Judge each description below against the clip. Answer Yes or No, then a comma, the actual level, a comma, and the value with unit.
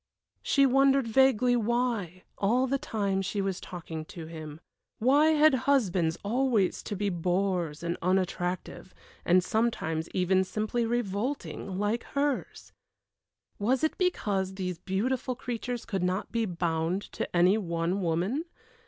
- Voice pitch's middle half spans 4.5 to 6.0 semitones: Yes, wide, 5.4 semitones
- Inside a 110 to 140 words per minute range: Yes, slow, 135 wpm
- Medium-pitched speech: No, high, 200 Hz